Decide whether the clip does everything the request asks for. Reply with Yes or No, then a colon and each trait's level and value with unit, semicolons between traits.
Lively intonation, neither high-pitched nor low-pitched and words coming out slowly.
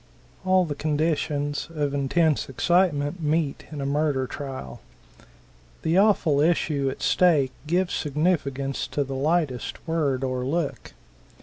No: average, 3.2 semitones; medium, 145 Hz; slow, 125 wpm